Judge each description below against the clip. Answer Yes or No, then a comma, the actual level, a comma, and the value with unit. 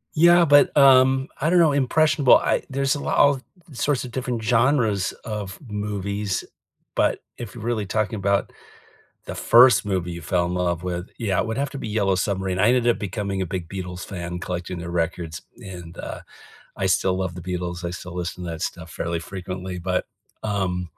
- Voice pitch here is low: Yes, very low, 95 Hz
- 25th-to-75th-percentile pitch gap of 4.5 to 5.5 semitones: Yes, average, 5.1 semitones